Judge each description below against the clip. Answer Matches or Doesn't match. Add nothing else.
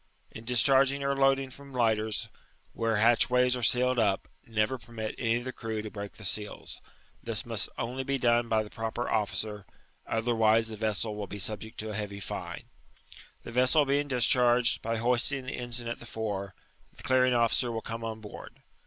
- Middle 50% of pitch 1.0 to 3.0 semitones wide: Matches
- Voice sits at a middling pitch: Doesn't match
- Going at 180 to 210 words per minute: Matches